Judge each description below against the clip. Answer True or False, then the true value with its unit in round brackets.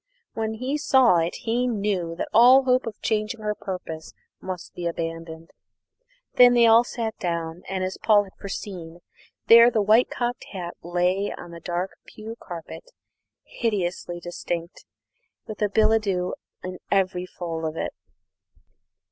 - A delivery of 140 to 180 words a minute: True (150 wpm)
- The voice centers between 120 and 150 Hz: False (195 Hz)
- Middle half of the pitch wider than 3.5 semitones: True (4.4 semitones)